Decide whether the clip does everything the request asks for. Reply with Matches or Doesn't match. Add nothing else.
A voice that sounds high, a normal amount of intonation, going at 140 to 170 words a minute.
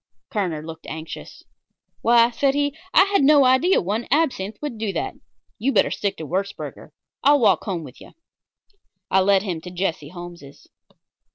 Doesn't match